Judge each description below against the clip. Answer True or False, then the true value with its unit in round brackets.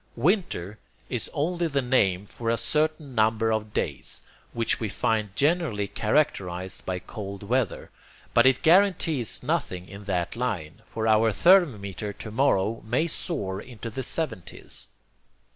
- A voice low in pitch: True (115 Hz)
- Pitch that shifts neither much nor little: False (5.9 semitones)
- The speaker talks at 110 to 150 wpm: True (140 wpm)